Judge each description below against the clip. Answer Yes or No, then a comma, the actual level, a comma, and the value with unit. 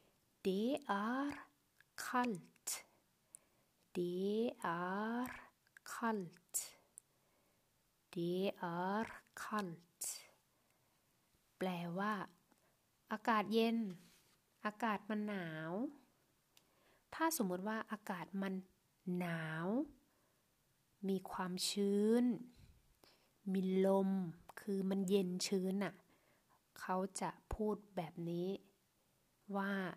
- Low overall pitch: No, high, 195 Hz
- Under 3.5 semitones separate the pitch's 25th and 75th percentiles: Yes, average, 3.0 semitones